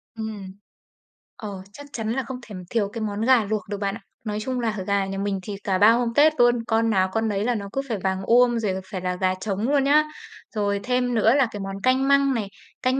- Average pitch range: Yes, average, 3.7 semitones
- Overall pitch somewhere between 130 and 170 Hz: No, high, 220 Hz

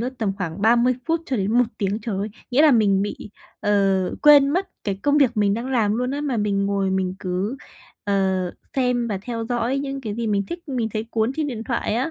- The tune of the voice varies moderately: Yes, average, 4.4 semitones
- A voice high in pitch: Yes, high, 230 Hz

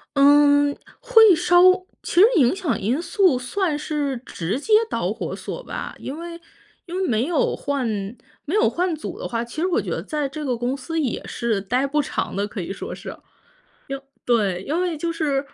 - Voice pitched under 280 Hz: No, very high, 290 Hz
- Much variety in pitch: Yes, wide, 5.7 semitones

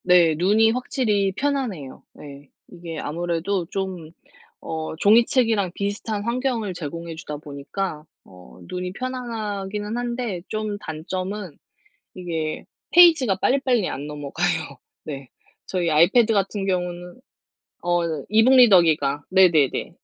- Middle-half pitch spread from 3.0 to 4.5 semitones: No, average, 5.2 semitones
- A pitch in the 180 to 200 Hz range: Yes, medium, 185 Hz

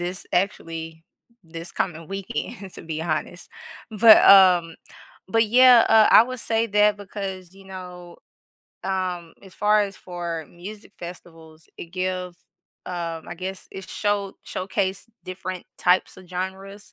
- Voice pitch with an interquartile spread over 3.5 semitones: No, narrow, 2.4 semitones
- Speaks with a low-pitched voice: No, medium, 185 Hz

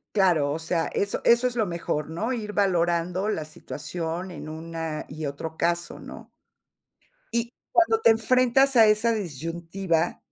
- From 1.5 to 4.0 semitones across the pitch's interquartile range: No, average, 5.3 semitones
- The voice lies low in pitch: No, medium, 175 Hz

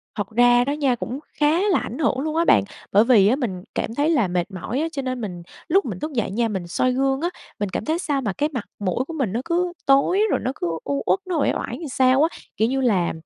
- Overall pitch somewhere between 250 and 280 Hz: Yes, very high, 255 Hz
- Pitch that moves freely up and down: Yes, wide, 5.9 semitones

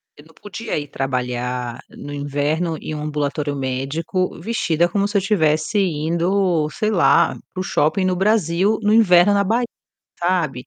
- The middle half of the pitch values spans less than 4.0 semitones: No, average, 5.0 semitones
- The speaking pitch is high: No, medium, 165 Hz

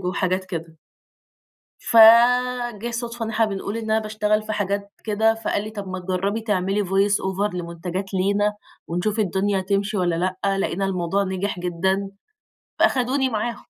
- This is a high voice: Yes, high, 200 Hz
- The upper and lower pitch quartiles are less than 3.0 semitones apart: Yes, narrow, 2.6 semitones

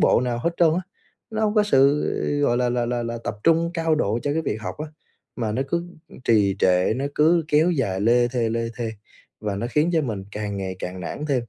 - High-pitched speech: No, low, 125 Hz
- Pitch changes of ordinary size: No, wide, 6.3 semitones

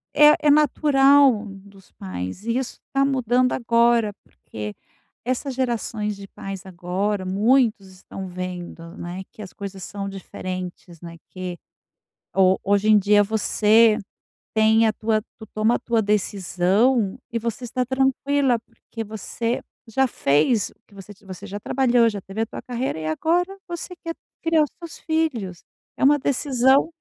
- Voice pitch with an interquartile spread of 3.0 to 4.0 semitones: No, average, 5.0 semitones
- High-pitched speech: Yes, high, 220 Hz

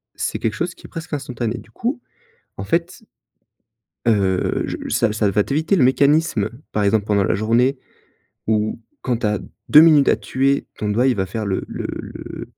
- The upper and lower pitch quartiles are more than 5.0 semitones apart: Yes, wide, 5.4 semitones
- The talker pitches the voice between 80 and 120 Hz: Yes, low, 115 Hz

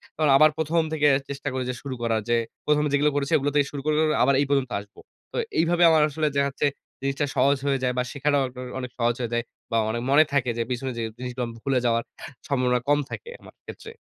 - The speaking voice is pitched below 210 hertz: Yes, medium, 140 Hz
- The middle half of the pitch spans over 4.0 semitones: No, average, 2.8 semitones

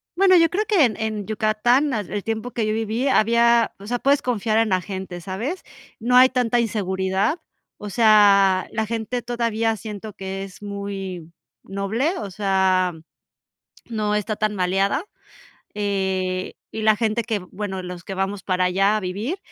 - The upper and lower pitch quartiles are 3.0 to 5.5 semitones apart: Yes, average, 3.3 semitones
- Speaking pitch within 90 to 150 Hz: No, high, 210 Hz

